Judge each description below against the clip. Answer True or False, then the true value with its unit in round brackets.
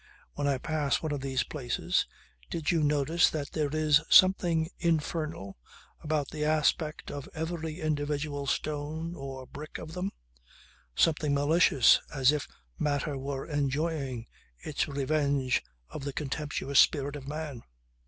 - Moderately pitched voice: True (150 Hz)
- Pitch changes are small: True (2.0 semitones)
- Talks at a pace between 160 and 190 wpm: False (135 wpm)